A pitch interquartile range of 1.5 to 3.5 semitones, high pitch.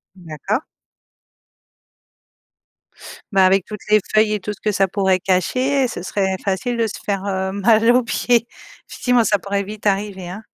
Yes: narrow, 2.5 semitones; high, 200 Hz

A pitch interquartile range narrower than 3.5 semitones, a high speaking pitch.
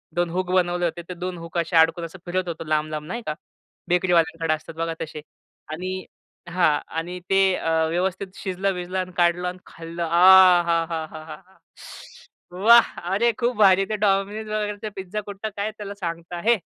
No: average, 2.7 semitones; medium, 180 Hz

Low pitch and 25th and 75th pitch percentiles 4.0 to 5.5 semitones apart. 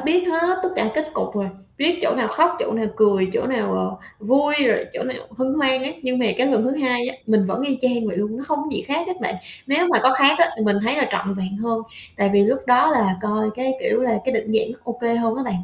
No: high, 245 Hz; average, 4.3 semitones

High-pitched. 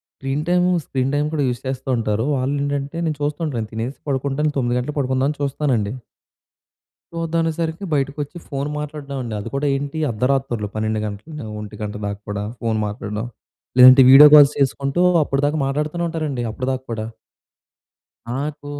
No: low, 135 Hz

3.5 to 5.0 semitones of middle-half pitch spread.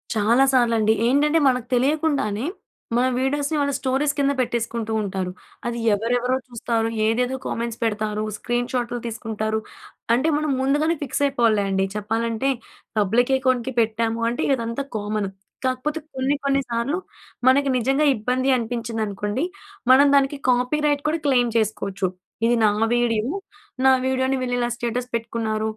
No: average, 3.1 semitones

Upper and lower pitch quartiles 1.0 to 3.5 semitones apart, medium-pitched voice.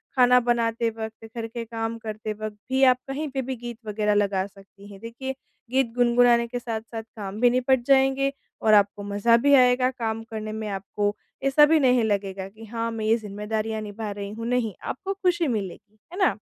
No: average, 2.8 semitones; high, 230 Hz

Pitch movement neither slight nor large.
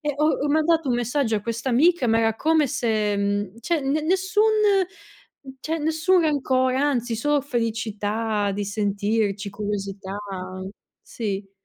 No: wide, 6.1 semitones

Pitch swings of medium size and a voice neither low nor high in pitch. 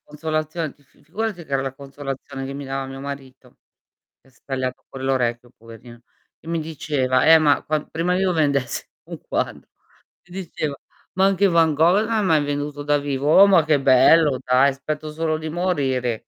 Yes: average, 3.3 semitones; medium, 145 Hz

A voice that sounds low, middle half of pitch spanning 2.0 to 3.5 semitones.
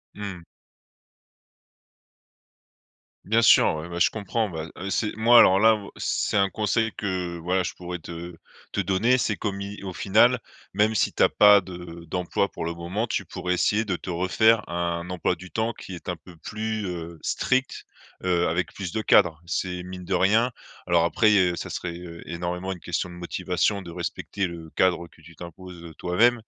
Yes: very low, 90 Hz; average, 3.2 semitones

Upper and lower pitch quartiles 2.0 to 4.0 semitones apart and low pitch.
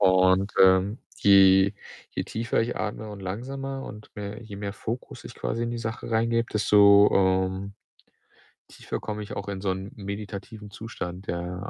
Yes: average, 2.7 semitones; low, 100 Hz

